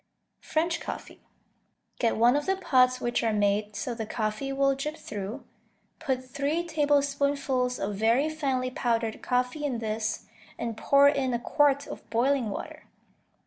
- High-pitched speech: Yes, very high, 255 Hz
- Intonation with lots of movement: No, average, 3.7 semitones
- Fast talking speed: No, average, 150 wpm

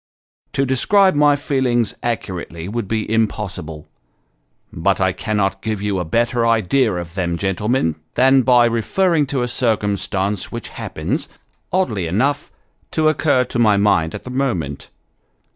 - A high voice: No, low, 115 Hz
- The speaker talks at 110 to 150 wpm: Yes, average, 145 wpm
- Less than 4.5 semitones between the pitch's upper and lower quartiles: No, average, 5.3 semitones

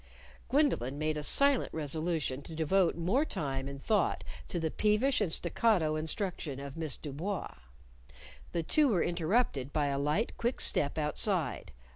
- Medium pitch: Yes, medium, 165 Hz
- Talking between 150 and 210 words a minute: Yes, average, 155 wpm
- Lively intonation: Yes, wide, 6.0 semitones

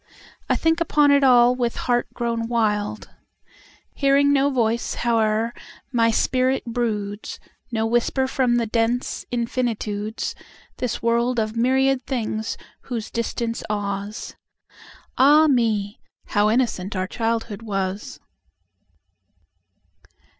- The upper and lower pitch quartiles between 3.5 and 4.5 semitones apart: No, average, 2.8 semitones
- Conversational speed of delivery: No, slow, 95 wpm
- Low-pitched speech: No, high, 235 Hz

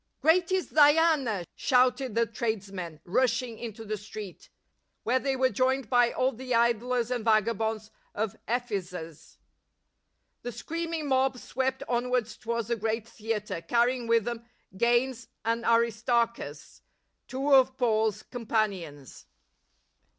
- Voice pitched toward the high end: Yes, high, 235 Hz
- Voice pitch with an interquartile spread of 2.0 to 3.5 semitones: Yes, average, 2.9 semitones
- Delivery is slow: Yes, slow, 130 wpm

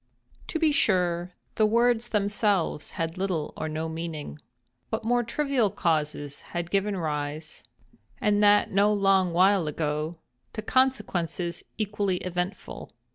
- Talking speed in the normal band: No, slow, 120 wpm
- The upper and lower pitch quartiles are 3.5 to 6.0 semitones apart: Yes, average, 4.5 semitones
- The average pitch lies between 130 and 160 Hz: No, medium, 185 Hz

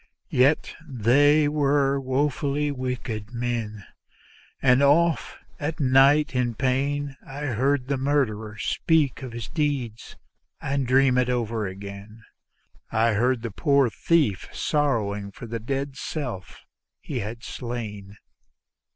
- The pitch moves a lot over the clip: No, average, 3.8 semitones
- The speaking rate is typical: No, slow, 120 wpm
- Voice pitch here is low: Yes, low, 130 Hz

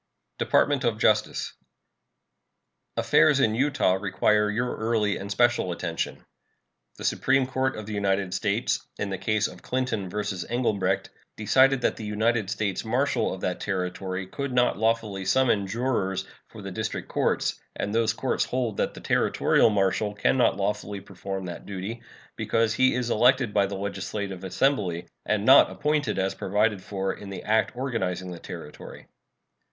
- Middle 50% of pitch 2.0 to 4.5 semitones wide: Yes, average, 3.8 semitones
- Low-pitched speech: Yes, low, 105 Hz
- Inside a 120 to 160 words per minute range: Yes, average, 155 wpm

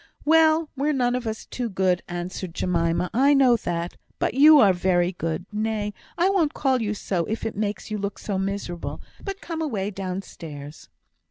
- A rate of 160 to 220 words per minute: Yes, average, 180 wpm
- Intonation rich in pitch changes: Yes, wide, 6.7 semitones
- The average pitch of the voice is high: Yes, high, 210 Hz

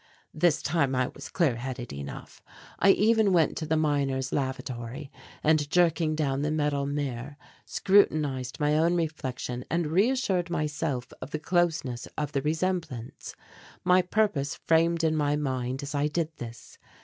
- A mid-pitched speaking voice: Yes, medium, 150 Hz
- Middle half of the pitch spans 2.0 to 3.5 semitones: No, average, 3.9 semitones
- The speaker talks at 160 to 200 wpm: No, average, 150 wpm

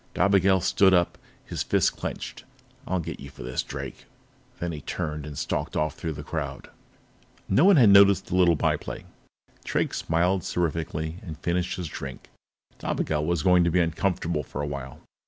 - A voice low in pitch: Yes, very low, 85 Hz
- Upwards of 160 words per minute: Yes, average, 175 wpm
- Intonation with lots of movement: No, average, 3.4 semitones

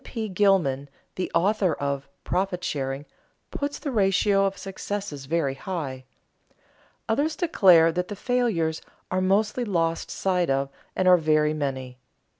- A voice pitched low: No, medium, 180 Hz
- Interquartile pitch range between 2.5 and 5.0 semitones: No, wide, 5.5 semitones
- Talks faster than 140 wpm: No, slow, 135 wpm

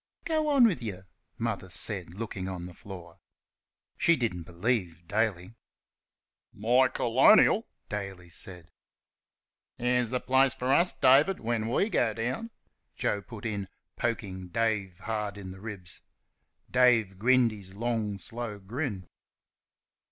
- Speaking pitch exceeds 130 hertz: No, low, 110 Hz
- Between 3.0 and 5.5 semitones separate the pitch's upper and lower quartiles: Yes, average, 4.6 semitones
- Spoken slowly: Yes, slow, 130 wpm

